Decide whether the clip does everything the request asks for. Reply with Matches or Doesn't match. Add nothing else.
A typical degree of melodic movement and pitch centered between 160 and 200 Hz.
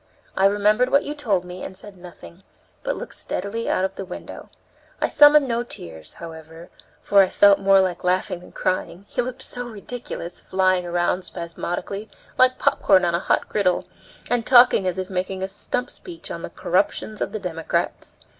Matches